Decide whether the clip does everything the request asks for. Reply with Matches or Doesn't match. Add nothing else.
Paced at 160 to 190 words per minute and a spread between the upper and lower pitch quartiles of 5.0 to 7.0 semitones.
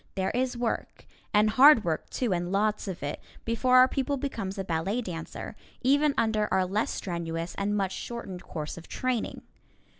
Matches